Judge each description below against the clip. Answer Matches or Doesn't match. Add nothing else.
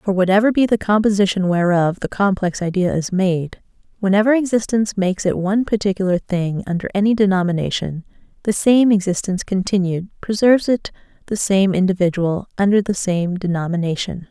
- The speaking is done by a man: Doesn't match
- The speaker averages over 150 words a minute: Doesn't match